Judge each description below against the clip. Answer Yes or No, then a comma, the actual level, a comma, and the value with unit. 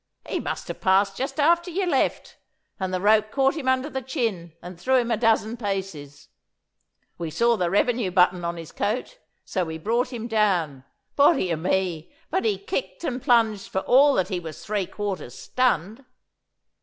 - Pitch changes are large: Yes, wide, 6.1 semitones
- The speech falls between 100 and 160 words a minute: No, average, 180 wpm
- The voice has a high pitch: Yes, high, 215 Hz